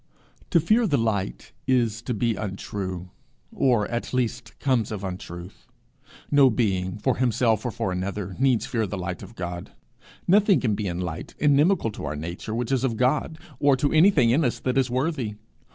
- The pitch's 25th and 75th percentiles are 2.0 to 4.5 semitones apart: No, wide, 5.5 semitones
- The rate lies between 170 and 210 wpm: Yes, average, 185 wpm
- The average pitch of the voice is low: Yes, low, 115 Hz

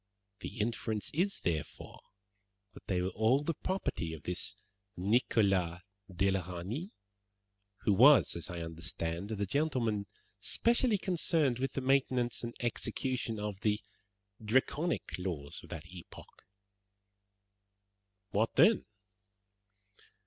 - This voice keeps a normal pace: No, slow, 115 wpm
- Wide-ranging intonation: Yes, wide, 6.7 semitones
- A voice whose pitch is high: No, low, 110 Hz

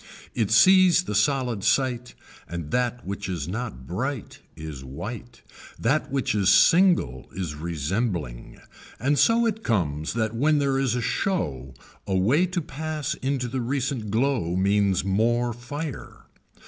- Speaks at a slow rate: No, average, 145 wpm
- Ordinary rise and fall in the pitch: No, wide, 6.8 semitones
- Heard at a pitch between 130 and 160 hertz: No, low, 115 Hz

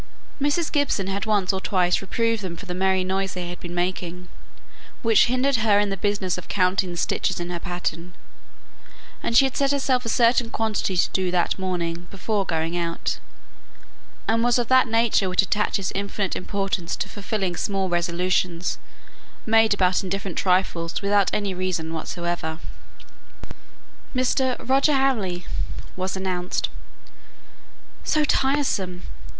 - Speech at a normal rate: Yes, average, 145 wpm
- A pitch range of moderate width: Yes, average, 3.9 semitones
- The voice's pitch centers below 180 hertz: No, high, 190 Hz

